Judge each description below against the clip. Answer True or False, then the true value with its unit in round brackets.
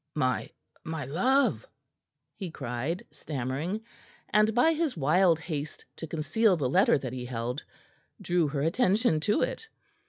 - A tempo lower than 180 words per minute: True (135 wpm)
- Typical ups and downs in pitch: False (7.2 semitones)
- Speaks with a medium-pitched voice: True (165 Hz)